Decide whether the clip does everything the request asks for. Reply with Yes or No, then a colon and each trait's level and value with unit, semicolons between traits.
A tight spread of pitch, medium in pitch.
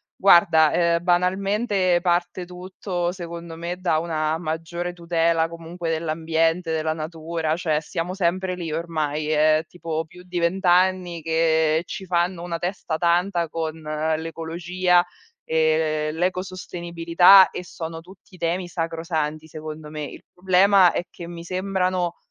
Yes: narrow, 2.0 semitones; medium, 170 Hz